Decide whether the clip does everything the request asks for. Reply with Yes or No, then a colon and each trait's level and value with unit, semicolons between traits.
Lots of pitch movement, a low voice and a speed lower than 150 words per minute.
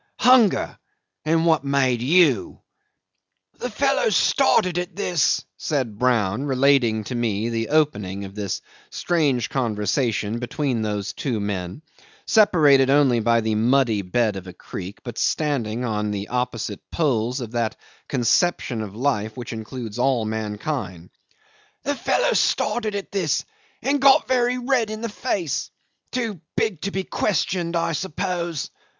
Yes: wide, 7.7 semitones; low, 130 Hz; average, 140 wpm